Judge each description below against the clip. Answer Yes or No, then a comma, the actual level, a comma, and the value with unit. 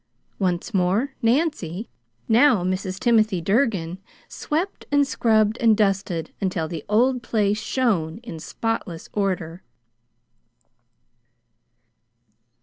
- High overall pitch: Yes, high, 210 Hz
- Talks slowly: Yes, slow, 95 wpm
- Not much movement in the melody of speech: No, average, 4.4 semitones